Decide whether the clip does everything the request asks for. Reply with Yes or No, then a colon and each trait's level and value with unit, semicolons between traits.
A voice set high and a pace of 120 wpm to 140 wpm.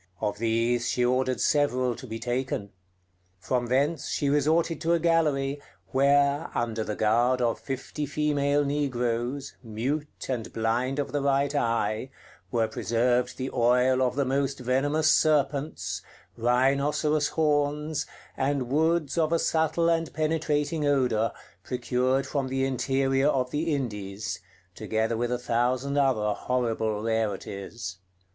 No: low, 130 Hz; slow, 135 wpm